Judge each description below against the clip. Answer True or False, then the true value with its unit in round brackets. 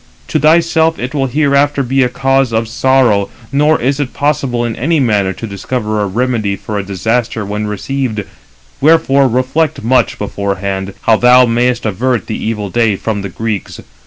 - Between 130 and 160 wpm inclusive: False (170 wpm)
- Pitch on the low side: True (120 Hz)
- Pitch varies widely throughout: False (4.4 semitones)